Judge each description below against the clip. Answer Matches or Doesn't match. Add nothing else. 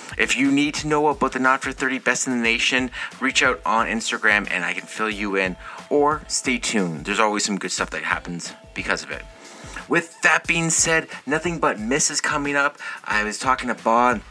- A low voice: Matches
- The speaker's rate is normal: Doesn't match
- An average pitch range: Doesn't match